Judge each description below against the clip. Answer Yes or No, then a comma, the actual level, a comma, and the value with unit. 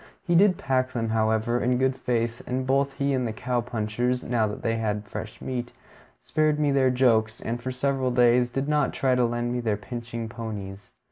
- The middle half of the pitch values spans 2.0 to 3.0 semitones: Yes, narrow, 2.4 semitones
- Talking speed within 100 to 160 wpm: No, fast, 205 wpm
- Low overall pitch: Yes, low, 120 Hz